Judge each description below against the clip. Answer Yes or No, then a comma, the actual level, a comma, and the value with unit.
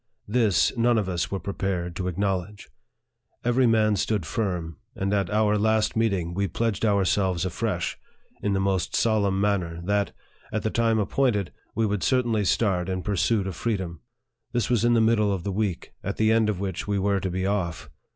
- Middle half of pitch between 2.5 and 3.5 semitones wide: Yes, average, 2.8 semitones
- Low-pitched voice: Yes, low, 100 Hz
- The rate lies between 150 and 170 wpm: No, average, 190 wpm